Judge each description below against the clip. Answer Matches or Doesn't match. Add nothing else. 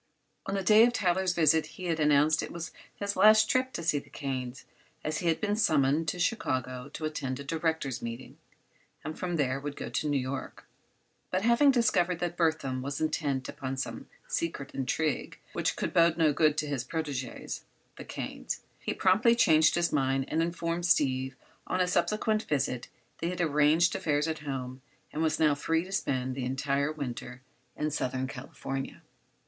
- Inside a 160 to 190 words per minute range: Matches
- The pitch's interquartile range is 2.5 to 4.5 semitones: Matches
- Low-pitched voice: Doesn't match